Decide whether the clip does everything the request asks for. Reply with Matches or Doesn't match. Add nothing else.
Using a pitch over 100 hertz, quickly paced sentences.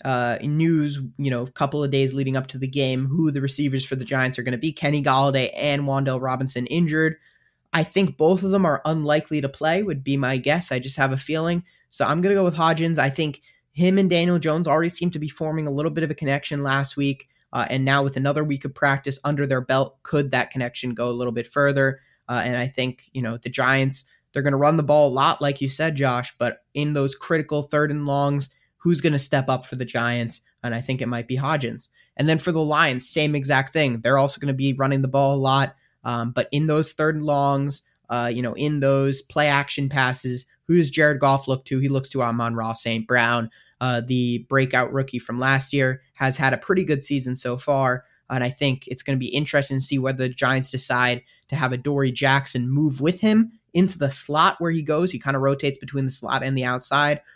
Matches